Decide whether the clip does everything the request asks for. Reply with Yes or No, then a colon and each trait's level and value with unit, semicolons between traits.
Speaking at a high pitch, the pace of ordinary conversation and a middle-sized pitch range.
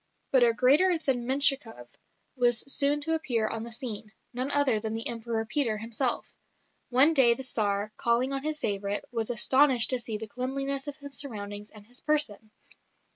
Yes: high, 245 Hz; average, 180 wpm; average, 3.8 semitones